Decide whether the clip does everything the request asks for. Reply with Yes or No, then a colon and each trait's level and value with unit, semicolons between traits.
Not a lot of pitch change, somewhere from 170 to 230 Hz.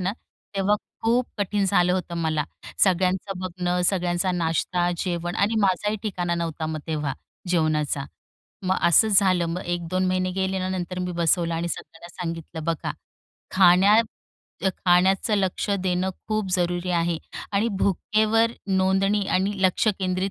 Yes: narrow, 2.0 semitones; medium, 185 Hz